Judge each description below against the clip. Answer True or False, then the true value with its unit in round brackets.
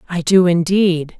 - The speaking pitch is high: False (175 Hz)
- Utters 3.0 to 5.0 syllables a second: True (4.3 syllables/s)